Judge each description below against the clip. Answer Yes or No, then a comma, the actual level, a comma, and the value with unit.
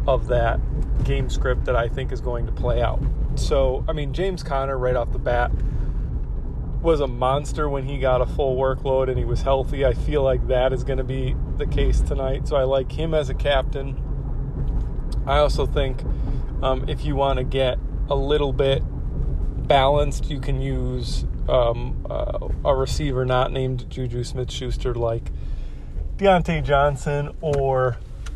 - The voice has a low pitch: Yes, low, 130 Hz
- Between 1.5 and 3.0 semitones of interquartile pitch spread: Yes, narrow, 2.4 semitones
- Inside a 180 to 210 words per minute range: No, average, 170 wpm